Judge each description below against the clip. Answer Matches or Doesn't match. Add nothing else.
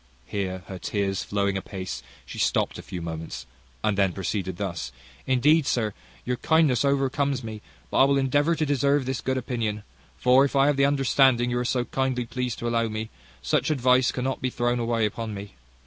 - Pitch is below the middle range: Matches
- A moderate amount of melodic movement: Matches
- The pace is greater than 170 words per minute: Matches